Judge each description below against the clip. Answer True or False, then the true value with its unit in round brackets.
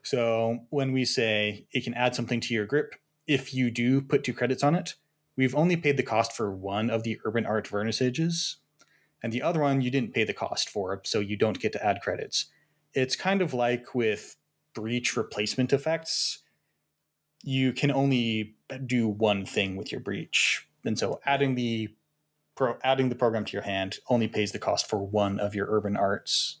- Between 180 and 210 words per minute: True (190 wpm)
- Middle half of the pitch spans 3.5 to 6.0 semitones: True (3.8 semitones)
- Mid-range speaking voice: False (120 Hz)